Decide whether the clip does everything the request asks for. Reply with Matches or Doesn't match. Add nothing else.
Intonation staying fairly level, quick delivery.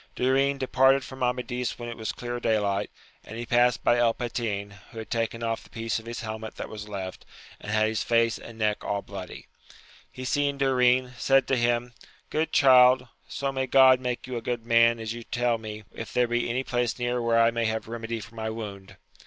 Matches